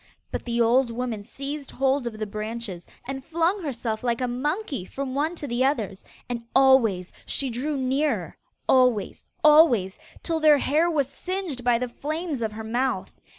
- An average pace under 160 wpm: No, average, 170 wpm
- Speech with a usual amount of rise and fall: Yes, average, 4.1 semitones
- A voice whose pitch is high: Yes, very high, 255 Hz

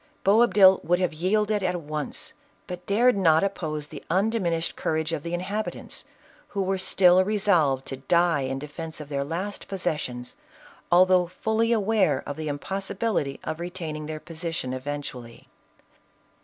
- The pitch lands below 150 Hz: No, medium, 175 Hz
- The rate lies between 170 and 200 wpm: No, average, 155 wpm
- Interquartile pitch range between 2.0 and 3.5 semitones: No, average, 4.2 semitones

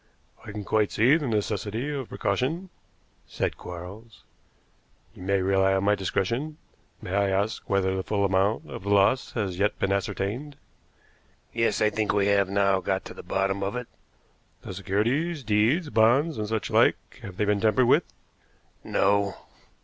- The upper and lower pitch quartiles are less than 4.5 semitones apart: Yes, average, 3.1 semitones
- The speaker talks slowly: No, average, 165 wpm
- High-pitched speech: No, low, 105 Hz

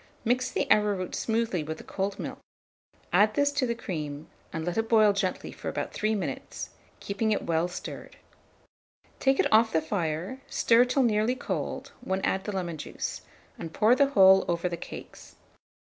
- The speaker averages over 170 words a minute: Yes, average, 180 wpm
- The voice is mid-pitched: No, high, 200 Hz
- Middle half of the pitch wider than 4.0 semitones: Yes, average, 4.8 semitones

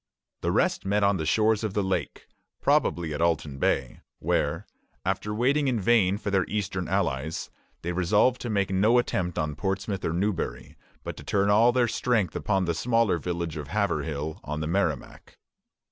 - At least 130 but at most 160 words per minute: No, average, 175 wpm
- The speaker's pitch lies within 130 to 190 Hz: No, very low, 95 Hz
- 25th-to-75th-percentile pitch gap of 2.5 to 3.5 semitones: No, average, 4.2 semitones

